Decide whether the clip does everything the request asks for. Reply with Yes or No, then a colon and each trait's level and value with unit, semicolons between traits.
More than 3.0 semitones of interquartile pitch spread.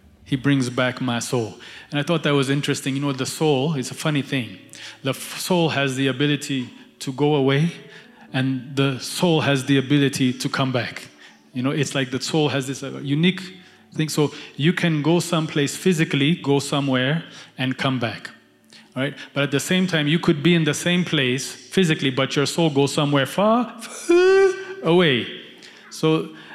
Yes: average, 3.5 semitones